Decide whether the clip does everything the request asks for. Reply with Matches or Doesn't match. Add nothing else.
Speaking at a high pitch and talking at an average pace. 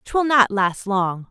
Matches